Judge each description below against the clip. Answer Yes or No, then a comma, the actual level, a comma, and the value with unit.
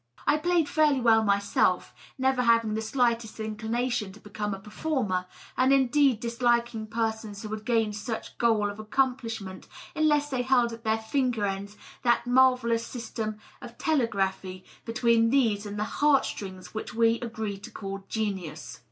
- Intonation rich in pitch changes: No, average, 3.0 semitones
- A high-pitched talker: Yes, high, 230 Hz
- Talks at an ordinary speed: Yes, average, 160 wpm